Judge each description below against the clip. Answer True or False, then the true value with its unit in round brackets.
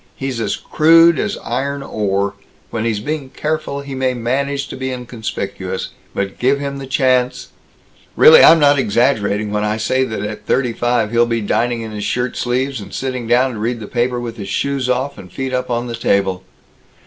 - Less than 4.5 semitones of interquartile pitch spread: True (3.3 semitones)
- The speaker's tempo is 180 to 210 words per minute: True (195 wpm)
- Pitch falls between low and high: False (125 Hz)